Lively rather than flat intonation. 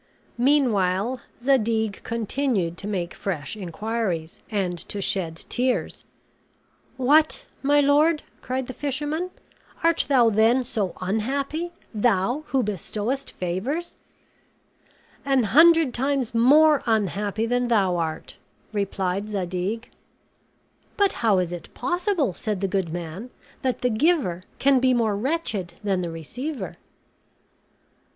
Yes: wide, 6.1 semitones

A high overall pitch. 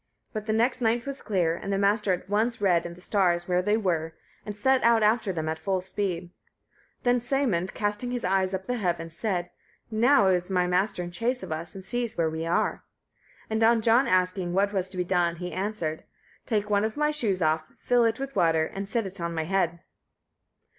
Yes: high, 195 Hz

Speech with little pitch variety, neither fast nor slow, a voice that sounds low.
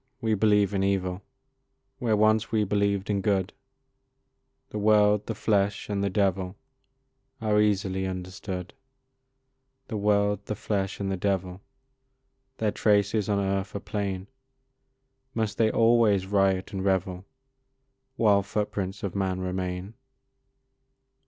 No: narrow, 1.7 semitones; slow, 125 wpm; low, 100 Hz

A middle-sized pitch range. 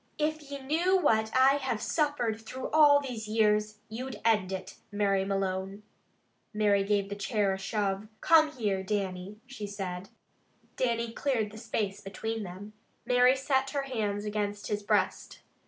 Yes: average, 4.5 semitones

